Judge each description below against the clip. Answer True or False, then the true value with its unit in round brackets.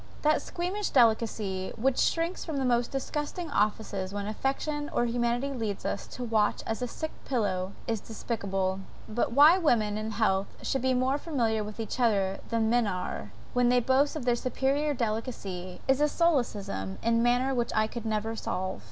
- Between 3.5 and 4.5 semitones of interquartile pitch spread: True (4.2 semitones)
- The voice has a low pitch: False (235 Hz)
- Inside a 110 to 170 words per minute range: False (180 wpm)